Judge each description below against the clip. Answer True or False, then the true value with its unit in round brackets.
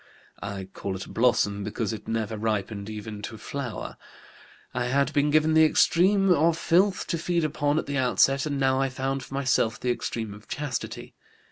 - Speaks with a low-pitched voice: True (130 Hz)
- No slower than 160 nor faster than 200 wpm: True (190 wpm)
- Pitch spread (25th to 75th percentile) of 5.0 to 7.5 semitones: True (5.4 semitones)